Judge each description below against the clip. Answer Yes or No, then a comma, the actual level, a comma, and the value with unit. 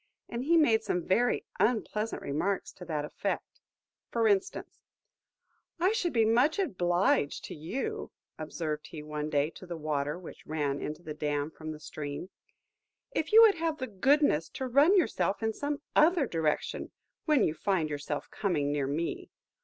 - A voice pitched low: No, medium, 185 Hz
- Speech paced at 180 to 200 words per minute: No, average, 165 wpm